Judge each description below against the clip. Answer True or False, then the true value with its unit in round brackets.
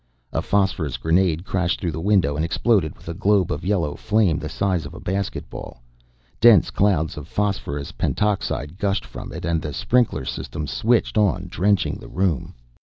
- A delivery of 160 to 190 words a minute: True (175 wpm)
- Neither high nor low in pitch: False (90 Hz)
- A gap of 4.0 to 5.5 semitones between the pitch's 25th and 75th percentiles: True (4.4 semitones)